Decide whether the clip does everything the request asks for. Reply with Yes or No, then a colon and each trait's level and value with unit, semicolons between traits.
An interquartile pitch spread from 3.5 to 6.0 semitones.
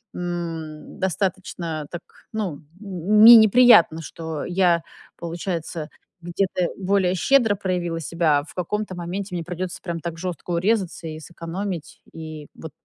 No: average, 2.7 semitones